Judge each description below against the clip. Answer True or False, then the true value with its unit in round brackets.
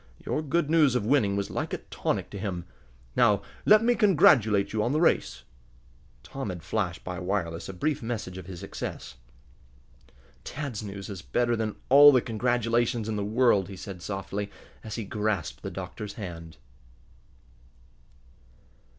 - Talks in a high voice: False (105 Hz)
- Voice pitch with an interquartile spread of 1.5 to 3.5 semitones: False (4.3 semitones)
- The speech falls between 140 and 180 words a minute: True (160 wpm)